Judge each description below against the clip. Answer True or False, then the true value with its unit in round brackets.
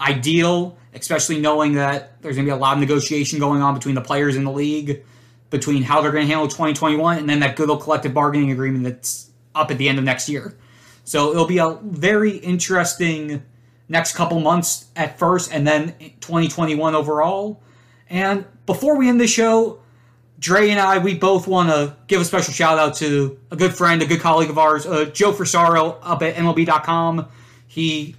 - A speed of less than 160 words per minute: False (195 wpm)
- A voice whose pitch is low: False (155 Hz)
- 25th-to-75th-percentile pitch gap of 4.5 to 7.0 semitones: False (3.3 semitones)